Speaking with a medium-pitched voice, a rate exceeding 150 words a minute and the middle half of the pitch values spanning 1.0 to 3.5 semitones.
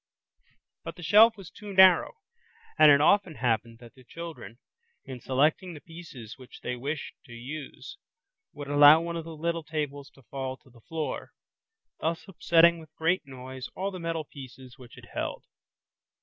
No: medium, 150 Hz; average, 170 wpm; average, 4.4 semitones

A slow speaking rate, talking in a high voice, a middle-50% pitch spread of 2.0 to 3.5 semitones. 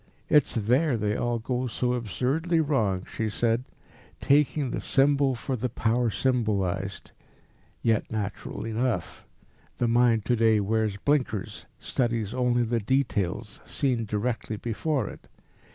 No: slow, 130 wpm; low, 115 Hz; average, 3.1 semitones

